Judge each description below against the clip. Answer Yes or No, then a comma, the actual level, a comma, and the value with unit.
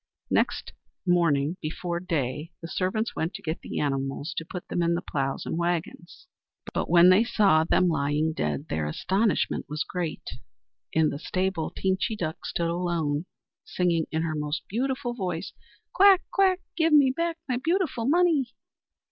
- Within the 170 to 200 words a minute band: No, average, 160 wpm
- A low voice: No, medium, 175 Hz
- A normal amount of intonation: No, wide, 6.3 semitones